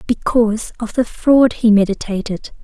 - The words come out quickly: No, slow, 135 wpm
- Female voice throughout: Yes, female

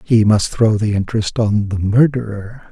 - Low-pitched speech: Yes, low, 110 Hz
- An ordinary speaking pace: Yes, average, 175 wpm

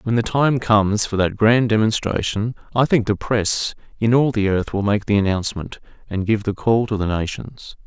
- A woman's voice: No, male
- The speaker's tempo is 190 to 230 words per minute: Yes, fast, 205 wpm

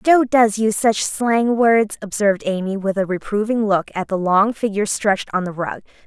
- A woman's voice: Yes, female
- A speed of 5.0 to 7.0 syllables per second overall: Yes, 5.1 syllables/s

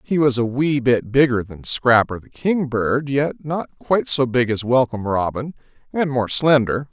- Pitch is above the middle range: No, low, 130 Hz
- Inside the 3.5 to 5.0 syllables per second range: Yes, 4.7 syllables/s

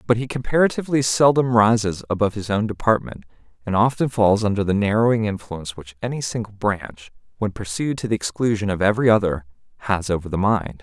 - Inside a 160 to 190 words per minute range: Yes, average, 175 wpm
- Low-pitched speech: Yes, low, 105 Hz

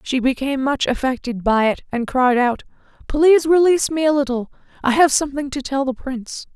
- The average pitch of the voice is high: Yes, very high, 270 Hz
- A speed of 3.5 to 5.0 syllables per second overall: No, 5.8 syllables/s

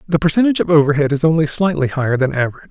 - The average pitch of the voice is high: No, medium, 155 Hz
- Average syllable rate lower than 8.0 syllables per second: No, 8.2 syllables/s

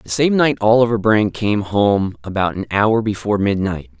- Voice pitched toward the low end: Yes, low, 105 Hz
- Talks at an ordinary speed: Yes, average, 180 wpm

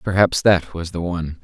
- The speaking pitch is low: Yes, very low, 90 Hz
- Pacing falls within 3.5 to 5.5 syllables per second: Yes, 5.3 syllables/s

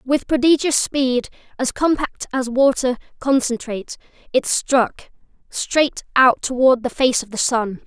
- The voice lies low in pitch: No, very high, 255 Hz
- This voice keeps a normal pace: No, slow, 130 wpm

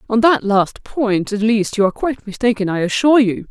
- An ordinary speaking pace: No, fast, 225 wpm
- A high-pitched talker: Yes, high, 220 Hz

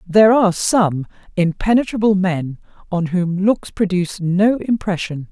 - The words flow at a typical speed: No, slow, 125 wpm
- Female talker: Yes, female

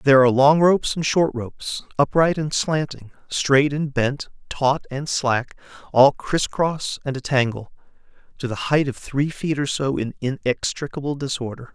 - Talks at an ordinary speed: Yes, average, 170 wpm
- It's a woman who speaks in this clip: No, male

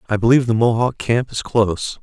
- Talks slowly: No, fast, 205 wpm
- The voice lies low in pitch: Yes, low, 115 Hz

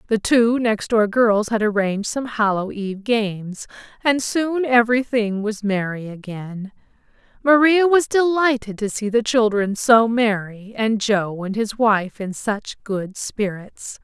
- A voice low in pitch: No, high, 220 Hz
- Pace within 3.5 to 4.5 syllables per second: Yes, 4.0 syllables/s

